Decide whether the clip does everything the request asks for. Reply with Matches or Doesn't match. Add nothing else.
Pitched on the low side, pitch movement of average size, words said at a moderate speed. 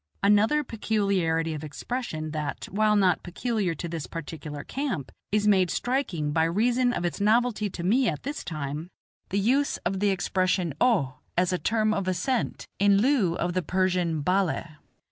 Doesn't match